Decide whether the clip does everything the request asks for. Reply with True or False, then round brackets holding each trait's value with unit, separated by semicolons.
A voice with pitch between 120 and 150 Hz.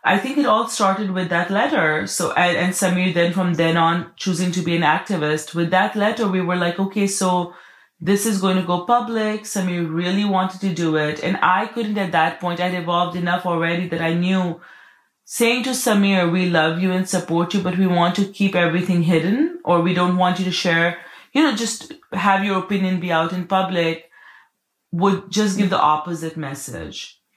False (180 Hz)